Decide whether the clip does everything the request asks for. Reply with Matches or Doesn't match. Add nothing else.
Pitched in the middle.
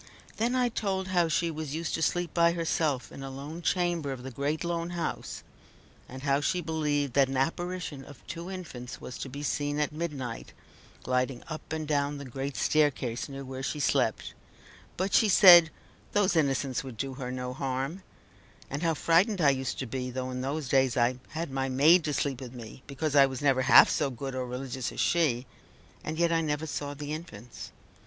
Matches